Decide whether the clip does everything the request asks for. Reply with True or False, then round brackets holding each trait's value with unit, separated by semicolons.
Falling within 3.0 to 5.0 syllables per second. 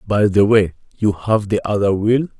True (4.7 syllables/s)